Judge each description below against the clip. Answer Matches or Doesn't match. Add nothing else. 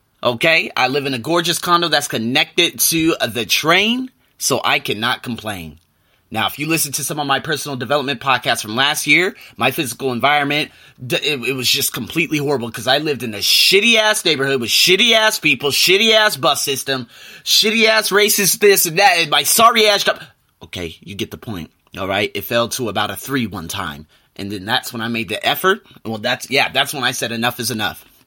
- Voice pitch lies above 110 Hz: Matches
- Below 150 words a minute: Doesn't match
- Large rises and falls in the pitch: Matches